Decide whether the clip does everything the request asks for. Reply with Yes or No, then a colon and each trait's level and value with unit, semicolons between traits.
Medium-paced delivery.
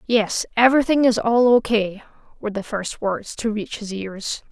Yes: average, 175 wpm